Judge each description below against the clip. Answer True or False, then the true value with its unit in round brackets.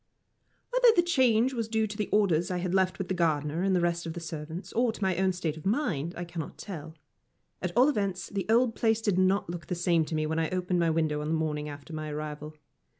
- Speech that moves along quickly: True (250 wpm)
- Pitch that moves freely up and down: False (4.6 semitones)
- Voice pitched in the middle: True (175 Hz)